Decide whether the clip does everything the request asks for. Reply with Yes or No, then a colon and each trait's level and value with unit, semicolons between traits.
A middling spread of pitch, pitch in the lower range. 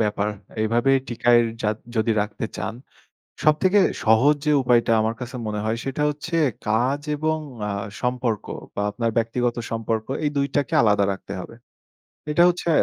Yes: average, 4.1 semitones; low, 120 Hz